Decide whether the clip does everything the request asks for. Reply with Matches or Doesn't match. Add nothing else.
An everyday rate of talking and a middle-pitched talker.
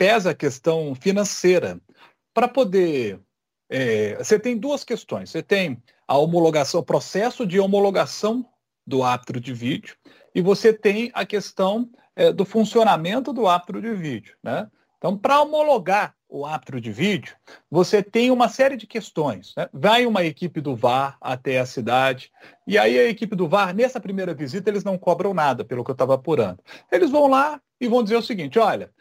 Doesn't match